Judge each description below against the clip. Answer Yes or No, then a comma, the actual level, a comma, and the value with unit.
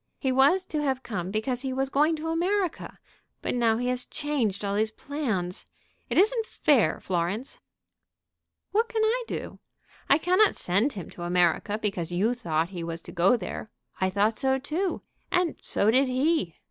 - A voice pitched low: No, very high, 250 Hz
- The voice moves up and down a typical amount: No, wide, 7.8 semitones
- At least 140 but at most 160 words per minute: No, average, 175 wpm